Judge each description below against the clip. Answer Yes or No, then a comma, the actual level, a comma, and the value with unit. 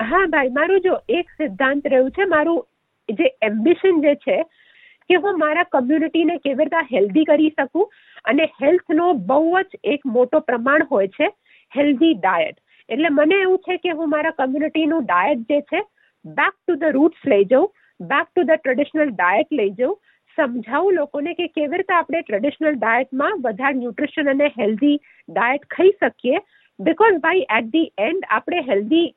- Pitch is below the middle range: No, very high, 310 Hz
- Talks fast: Yes, fast, 165 wpm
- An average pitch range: Yes, average, 3.5 semitones